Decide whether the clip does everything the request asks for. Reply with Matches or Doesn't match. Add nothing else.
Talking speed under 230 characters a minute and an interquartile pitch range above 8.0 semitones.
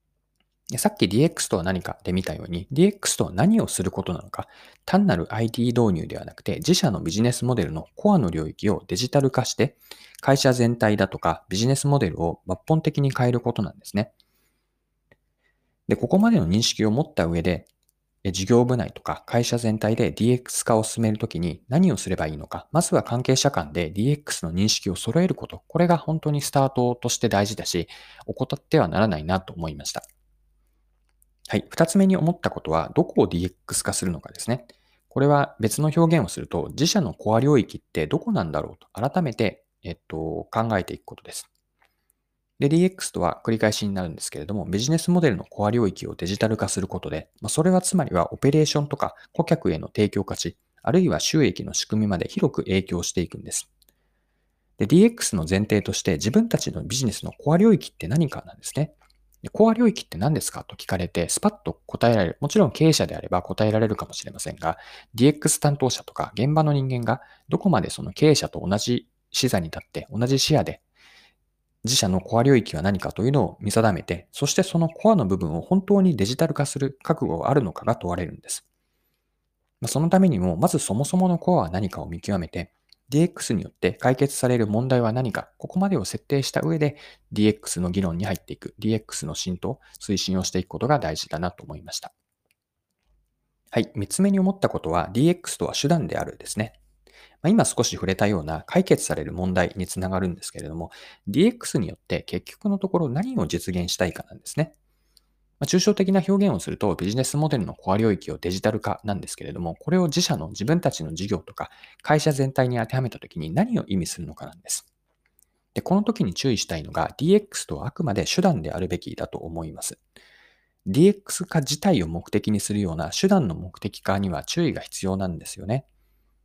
Doesn't match